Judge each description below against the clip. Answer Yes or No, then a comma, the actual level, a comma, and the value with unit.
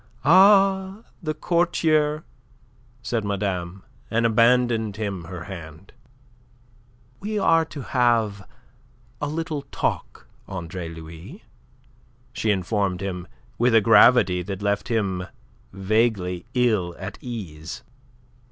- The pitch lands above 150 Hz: No, low, 110 Hz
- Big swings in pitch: Yes, wide, 6.1 semitones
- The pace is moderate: No, slow, 105 wpm